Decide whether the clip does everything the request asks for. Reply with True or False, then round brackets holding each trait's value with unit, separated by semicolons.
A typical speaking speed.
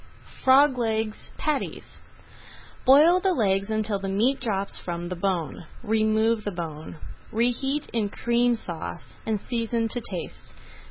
False (130 wpm)